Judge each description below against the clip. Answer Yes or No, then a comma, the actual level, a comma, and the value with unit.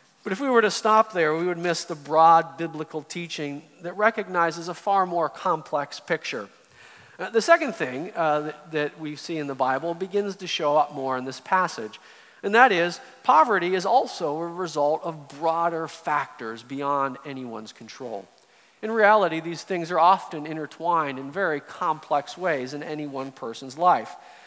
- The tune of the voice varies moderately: Yes, average, 3.5 semitones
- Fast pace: No, average, 175 wpm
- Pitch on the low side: No, medium, 165 Hz